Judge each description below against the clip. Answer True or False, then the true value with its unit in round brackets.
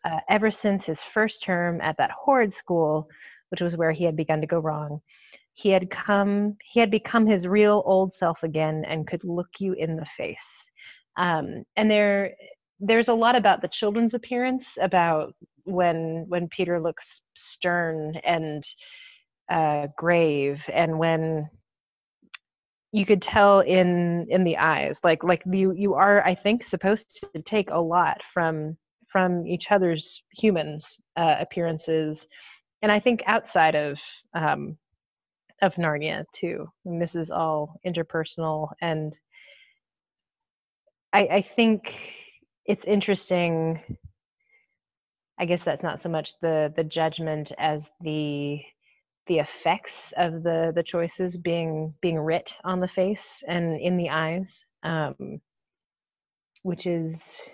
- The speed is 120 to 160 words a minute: True (140 wpm)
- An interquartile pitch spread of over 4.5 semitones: False (3.9 semitones)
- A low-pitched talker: False (175 Hz)